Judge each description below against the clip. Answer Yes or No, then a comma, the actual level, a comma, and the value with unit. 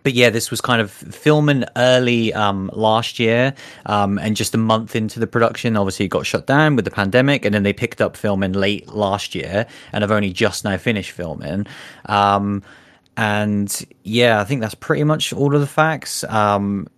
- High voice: No, low, 110 Hz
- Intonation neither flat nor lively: Yes, average, 3.4 semitones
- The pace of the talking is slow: No, average, 200 wpm